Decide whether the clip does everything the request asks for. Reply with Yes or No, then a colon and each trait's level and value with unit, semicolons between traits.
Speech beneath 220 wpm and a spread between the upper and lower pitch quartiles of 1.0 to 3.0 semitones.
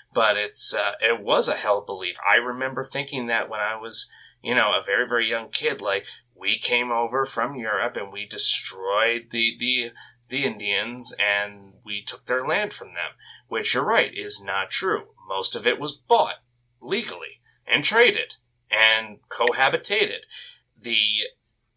Yes: average, 170 wpm; average, 2.7 semitones